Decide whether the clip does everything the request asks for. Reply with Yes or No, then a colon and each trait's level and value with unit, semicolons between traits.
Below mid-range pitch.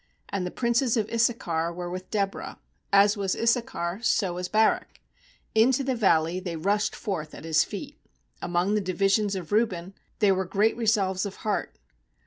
No: high, 200 Hz